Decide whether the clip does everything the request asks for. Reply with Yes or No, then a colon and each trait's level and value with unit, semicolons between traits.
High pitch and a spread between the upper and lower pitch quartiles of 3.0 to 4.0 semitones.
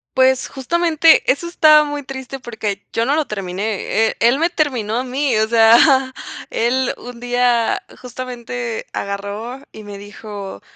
Yes: high, 245 Hz; average, 3.5 semitones